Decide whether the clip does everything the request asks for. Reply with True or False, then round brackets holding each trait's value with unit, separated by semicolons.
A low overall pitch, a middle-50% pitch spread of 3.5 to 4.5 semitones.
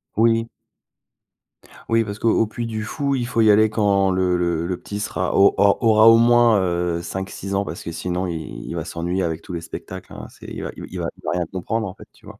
True (100 Hz; 4.2 semitones)